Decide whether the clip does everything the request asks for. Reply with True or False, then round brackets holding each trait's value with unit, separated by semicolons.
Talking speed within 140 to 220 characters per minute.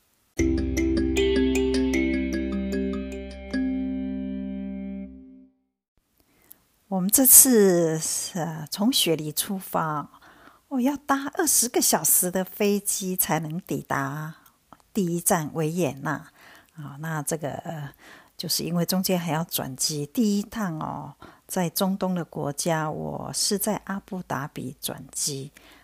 True (150 characters per minute)